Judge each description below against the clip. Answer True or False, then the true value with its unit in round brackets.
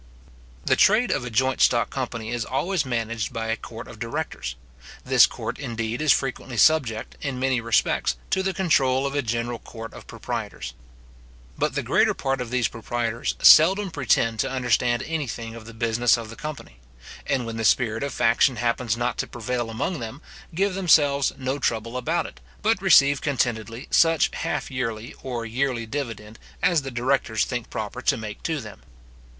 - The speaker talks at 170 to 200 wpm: True (180 wpm)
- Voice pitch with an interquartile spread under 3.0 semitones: False (3.4 semitones)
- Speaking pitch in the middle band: False (125 Hz)